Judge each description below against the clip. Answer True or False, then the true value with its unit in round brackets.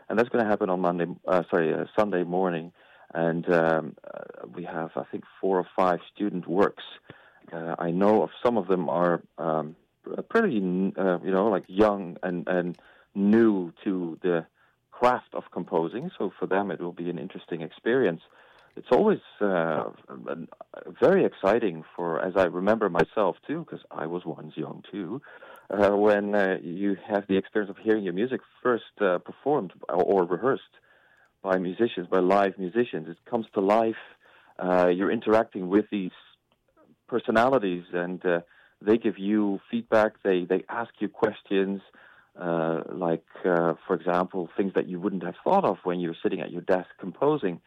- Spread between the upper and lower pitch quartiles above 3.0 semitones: False (2.7 semitones)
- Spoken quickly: False (170 wpm)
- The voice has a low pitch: True (90 Hz)